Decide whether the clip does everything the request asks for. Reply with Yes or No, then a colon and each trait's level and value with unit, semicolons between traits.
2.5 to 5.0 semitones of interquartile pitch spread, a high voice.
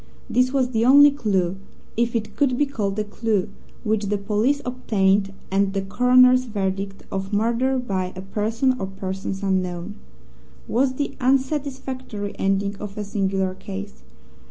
Yes: average, 4.6 semitones; high, 210 Hz